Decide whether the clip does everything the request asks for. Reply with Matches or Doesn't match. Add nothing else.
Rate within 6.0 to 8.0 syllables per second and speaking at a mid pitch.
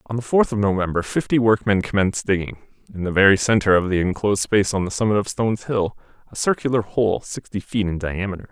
Doesn't match